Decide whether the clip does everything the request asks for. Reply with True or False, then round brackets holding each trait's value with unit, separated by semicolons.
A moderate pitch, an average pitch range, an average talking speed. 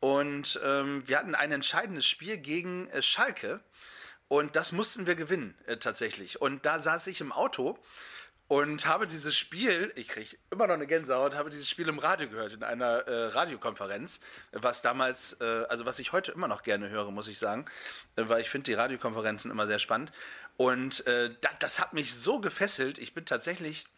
False (145 Hz; 4.0 semitones; 195 wpm)